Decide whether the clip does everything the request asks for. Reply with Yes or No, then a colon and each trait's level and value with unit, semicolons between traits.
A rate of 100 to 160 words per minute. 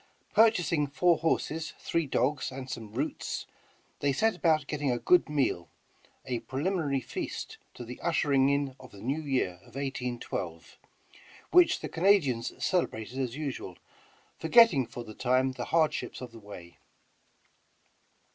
Yes: average, 140 wpm